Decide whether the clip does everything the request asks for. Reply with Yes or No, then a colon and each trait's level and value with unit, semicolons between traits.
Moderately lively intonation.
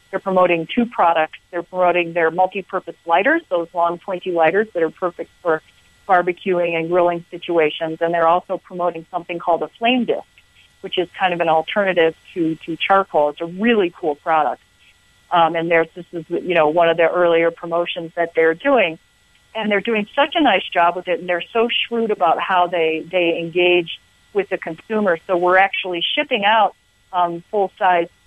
No: narrow, 2.1 semitones